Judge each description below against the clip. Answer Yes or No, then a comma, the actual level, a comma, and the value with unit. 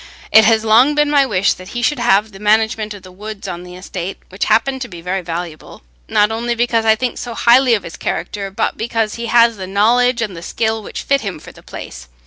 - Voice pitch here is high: Yes, high, 220 Hz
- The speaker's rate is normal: No, fast, 240 wpm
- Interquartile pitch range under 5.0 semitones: Yes, average, 3.7 semitones